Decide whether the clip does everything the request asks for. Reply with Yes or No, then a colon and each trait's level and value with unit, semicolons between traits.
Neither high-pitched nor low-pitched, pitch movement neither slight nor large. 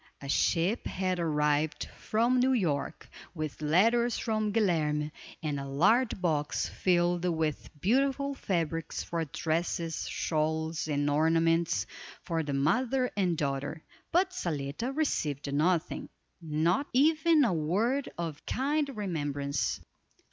No: medium, 165 Hz; wide, 7.2 semitones